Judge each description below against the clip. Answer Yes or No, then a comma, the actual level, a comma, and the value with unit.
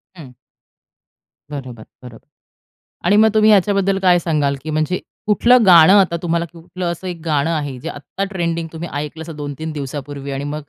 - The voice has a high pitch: No, medium, 165 Hz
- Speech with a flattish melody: No, average, 4.0 semitones